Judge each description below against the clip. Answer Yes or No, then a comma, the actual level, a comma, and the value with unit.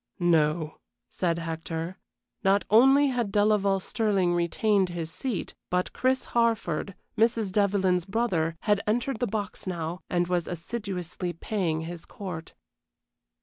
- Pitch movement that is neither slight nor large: Yes, average, 3.9 semitones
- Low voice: No, high, 190 Hz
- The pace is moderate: No, slow, 125 wpm